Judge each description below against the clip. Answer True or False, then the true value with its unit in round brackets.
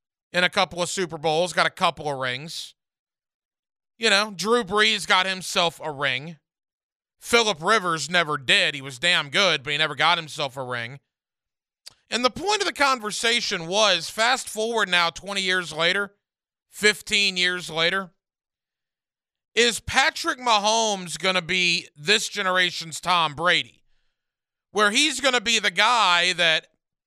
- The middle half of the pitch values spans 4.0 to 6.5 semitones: True (4.5 semitones)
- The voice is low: False (185 Hz)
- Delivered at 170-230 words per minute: False (150 wpm)